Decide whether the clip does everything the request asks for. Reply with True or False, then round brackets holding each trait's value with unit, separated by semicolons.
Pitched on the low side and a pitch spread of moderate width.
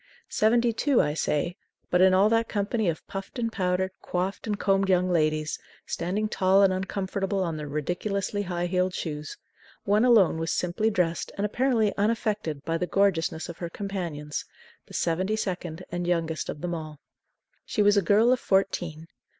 False (185 Hz; 3.4 semitones)